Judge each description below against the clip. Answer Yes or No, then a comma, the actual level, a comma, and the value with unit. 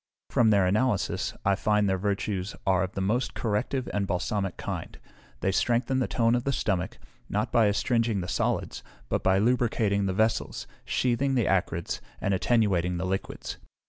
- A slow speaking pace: No, average, 170 wpm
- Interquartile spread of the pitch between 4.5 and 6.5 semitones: No, average, 3.6 semitones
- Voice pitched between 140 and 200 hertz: No, low, 105 Hz